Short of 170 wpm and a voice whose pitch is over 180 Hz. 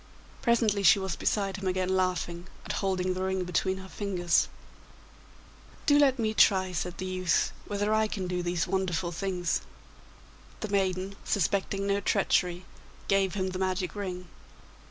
Yes: average, 155 wpm; high, 190 Hz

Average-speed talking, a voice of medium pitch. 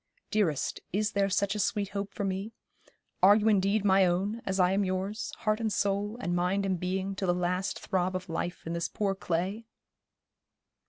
No: average, 195 wpm; high, 195 Hz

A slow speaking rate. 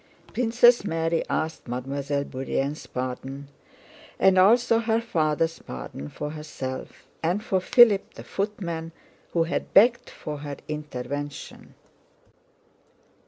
Yes: slow, 110 wpm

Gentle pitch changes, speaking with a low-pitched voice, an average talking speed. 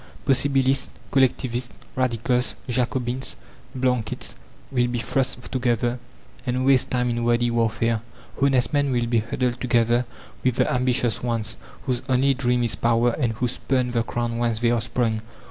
Yes: narrow, 1.5 semitones; low, 120 Hz; average, 150 wpm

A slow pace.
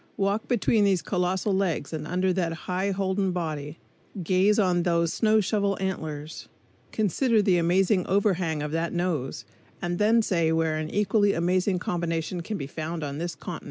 No: average, 165 wpm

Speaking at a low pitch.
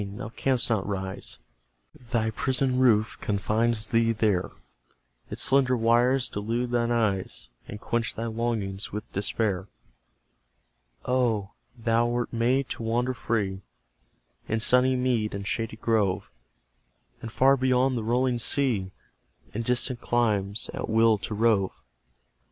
Yes: low, 115 Hz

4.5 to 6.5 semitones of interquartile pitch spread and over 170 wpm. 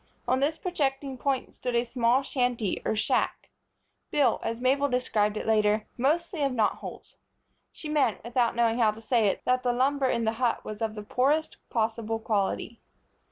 No: average, 3.3 semitones; average, 180 wpm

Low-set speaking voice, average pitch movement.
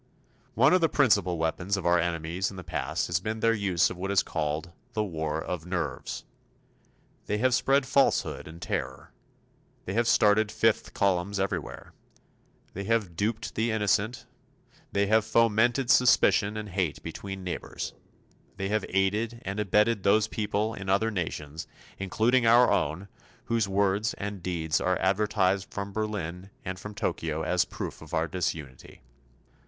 Yes: low, 100 Hz; average, 3.7 semitones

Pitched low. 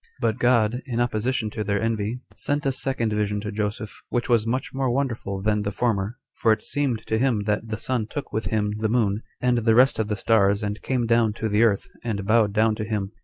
Yes: low, 110 Hz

